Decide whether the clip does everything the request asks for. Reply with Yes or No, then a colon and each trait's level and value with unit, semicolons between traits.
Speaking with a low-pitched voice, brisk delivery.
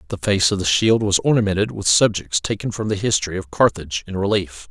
Yes: low, 100 Hz; fast, 215 wpm